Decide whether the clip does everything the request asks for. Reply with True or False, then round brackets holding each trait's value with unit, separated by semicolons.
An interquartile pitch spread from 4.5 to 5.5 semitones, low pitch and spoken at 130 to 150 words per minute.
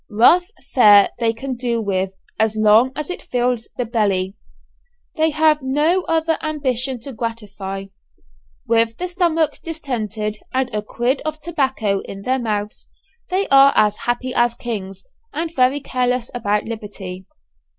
False (5.1 semitones; 240 Hz; 145 wpm)